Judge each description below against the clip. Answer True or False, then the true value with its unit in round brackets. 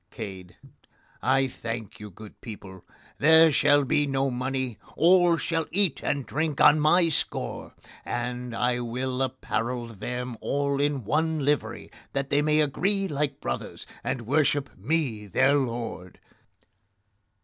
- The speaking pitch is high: False (135 Hz)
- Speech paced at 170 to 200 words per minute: False (135 wpm)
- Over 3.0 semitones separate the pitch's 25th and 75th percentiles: True (4.0 semitones)